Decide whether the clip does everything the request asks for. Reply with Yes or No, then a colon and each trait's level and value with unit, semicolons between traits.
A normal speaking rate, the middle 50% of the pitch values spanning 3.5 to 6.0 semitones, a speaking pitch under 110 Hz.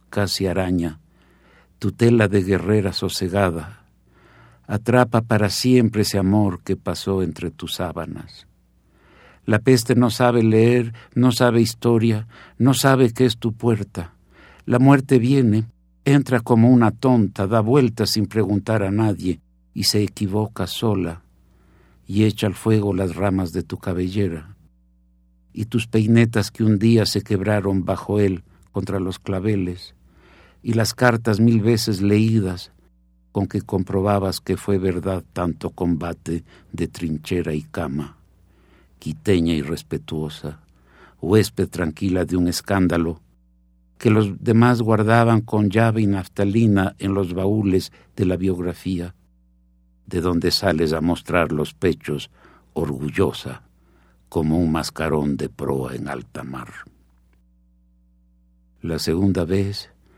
Yes: average, 130 wpm; average, 4.7 semitones; very low, 95 Hz